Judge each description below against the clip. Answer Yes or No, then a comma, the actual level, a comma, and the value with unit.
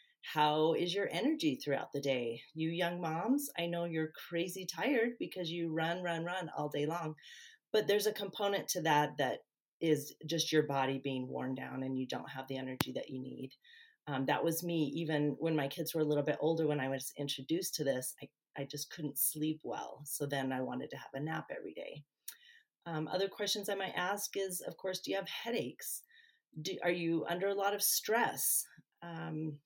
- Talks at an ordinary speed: No, fast, 210 wpm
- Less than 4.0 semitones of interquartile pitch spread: No, average, 5.0 semitones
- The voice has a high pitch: No, medium, 165 Hz